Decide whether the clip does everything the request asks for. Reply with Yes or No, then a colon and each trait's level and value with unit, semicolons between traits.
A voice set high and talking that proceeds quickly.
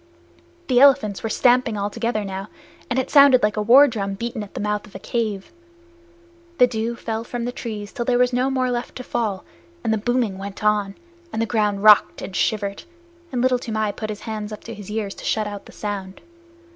Yes: high, 220 Hz; fast, 220 wpm